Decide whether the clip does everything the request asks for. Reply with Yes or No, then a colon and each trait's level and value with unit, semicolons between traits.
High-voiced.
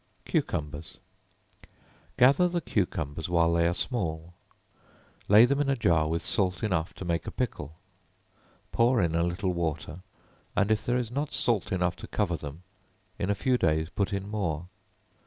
No: very low, 90 Hz